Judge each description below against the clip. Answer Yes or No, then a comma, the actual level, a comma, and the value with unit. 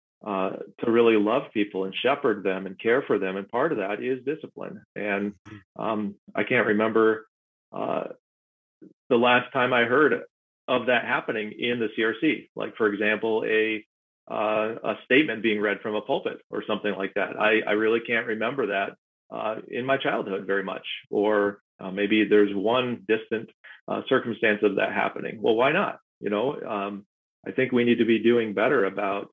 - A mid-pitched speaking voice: No, low, 110 Hz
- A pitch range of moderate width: No, narrow, 2.0 semitones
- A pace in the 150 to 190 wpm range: Yes, average, 180 wpm